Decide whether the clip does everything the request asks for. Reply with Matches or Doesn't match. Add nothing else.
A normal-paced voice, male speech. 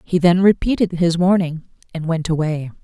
Doesn't match